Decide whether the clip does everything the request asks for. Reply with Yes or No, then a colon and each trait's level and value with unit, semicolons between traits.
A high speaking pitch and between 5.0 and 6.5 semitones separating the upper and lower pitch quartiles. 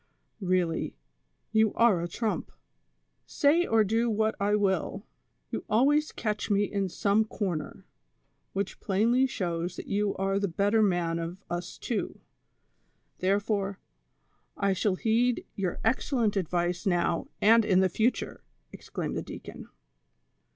No: high, 200 Hz; average, 3.2 semitones